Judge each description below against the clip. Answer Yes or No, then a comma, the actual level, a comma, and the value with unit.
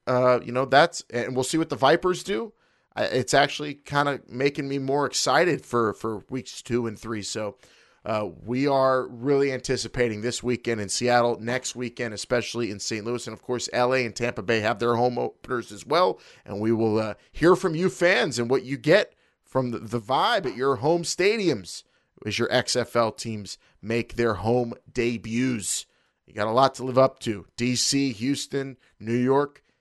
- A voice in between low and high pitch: No, low, 125 Hz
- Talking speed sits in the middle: Yes, average, 190 wpm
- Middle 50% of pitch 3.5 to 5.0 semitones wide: No, average, 3.0 semitones